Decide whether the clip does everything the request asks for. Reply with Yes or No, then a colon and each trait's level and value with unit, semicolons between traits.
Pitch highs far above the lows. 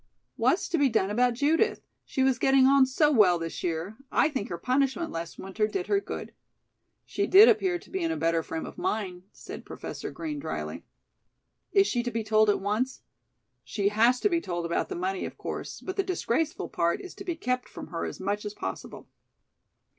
Yes: wide, 8.3 semitones